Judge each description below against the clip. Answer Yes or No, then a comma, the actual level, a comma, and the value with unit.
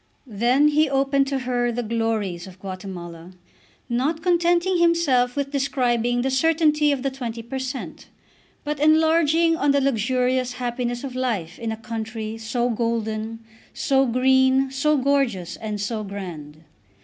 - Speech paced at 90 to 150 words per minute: Yes, average, 145 wpm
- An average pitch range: Yes, average, 3.7 semitones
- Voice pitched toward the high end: Yes, very high, 250 Hz